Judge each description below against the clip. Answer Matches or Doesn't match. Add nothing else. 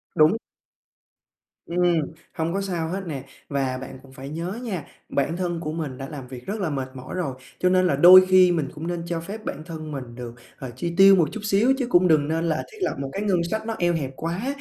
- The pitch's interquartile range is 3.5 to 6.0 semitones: Matches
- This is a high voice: Doesn't match